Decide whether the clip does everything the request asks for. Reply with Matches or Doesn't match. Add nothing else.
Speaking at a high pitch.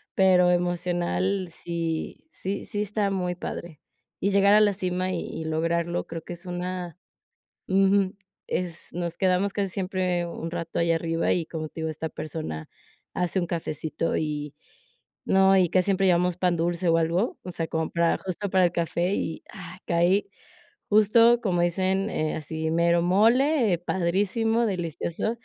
Doesn't match